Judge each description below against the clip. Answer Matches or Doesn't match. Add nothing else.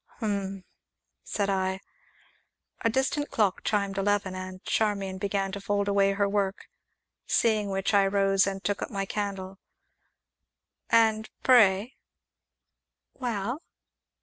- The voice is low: Doesn't match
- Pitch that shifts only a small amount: Matches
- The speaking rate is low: Matches